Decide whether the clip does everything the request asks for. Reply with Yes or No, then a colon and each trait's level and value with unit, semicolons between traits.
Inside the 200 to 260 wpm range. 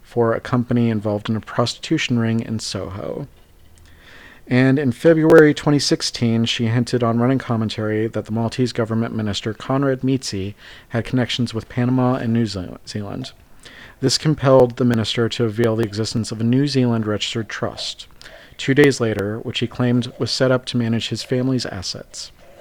No: average, 165 wpm